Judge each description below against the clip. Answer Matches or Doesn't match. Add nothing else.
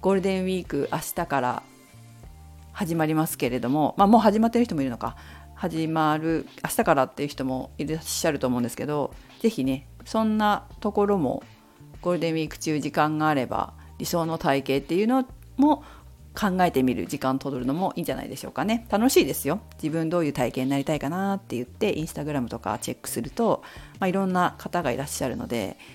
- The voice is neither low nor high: Matches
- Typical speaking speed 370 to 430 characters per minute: Matches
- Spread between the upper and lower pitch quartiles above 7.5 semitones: Doesn't match